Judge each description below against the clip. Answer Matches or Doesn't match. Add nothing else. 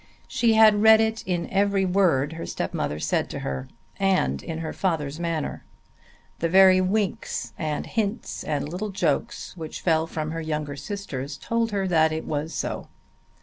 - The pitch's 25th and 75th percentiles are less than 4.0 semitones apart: Doesn't match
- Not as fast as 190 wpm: Matches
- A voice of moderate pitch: Matches